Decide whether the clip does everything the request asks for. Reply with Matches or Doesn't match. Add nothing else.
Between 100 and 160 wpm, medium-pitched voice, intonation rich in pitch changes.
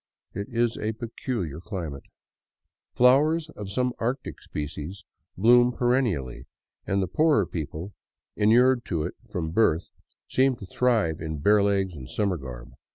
Doesn't match